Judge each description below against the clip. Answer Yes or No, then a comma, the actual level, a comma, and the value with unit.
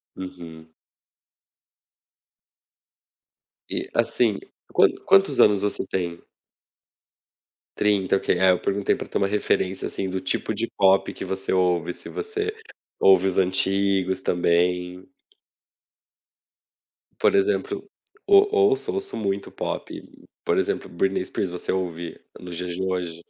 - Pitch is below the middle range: Yes, very low, 95 Hz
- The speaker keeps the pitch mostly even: Yes, narrow, 2.3 semitones